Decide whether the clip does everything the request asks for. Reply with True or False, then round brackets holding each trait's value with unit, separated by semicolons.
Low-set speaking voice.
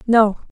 False (220 Hz)